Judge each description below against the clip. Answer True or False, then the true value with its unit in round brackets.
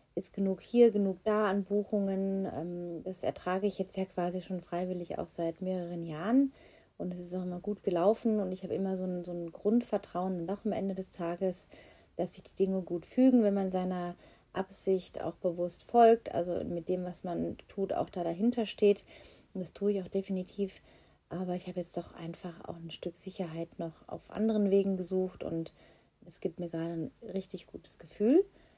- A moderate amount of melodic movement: False (2.3 semitones)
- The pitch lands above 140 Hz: True (185 Hz)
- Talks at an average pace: False (195 wpm)